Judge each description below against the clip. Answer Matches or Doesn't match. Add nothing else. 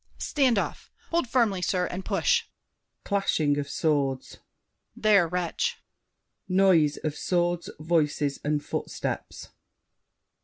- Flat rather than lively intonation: Doesn't match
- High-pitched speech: Doesn't match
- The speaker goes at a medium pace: Doesn't match